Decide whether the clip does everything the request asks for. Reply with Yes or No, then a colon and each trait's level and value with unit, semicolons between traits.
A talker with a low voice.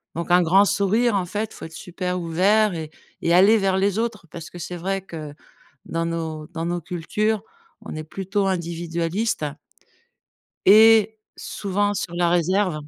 No: medium, 180 Hz